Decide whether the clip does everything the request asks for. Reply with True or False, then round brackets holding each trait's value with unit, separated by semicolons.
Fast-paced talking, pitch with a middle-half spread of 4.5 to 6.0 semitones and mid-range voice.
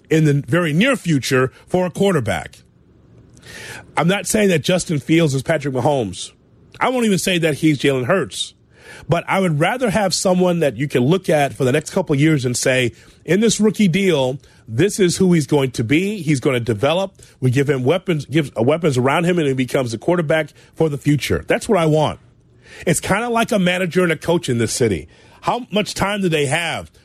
True (215 wpm; 5.0 semitones; 155 Hz)